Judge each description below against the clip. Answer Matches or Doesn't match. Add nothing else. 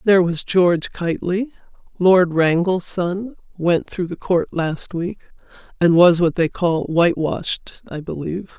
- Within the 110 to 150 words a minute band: Matches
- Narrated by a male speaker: Doesn't match